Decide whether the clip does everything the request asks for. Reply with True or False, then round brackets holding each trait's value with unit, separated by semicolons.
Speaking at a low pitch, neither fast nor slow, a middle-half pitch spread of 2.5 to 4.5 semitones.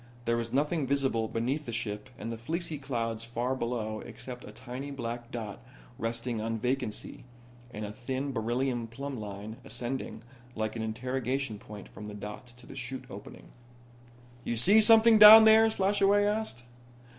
True (120 Hz; 160 wpm; 3.5 semitones)